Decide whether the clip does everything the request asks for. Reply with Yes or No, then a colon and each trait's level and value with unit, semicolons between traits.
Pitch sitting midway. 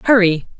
No: high, 195 Hz